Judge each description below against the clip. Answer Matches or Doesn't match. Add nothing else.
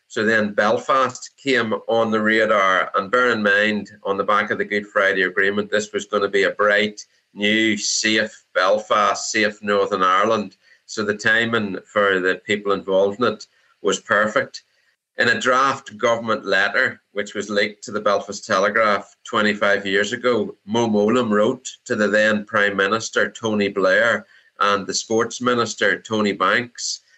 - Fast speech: Doesn't match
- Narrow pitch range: Matches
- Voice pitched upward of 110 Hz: Doesn't match